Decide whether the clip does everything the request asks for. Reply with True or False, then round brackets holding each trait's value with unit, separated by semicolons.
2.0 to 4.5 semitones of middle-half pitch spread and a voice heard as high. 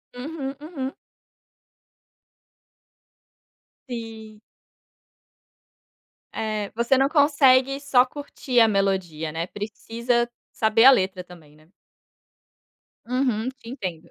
False (5.1 semitones; 230 Hz)